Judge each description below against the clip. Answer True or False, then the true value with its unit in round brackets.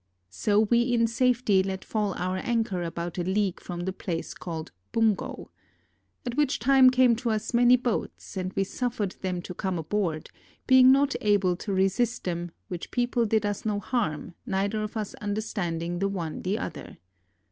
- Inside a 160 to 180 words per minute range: True (175 wpm)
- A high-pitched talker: True (205 Hz)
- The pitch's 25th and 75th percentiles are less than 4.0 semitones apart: False (4.3 semitones)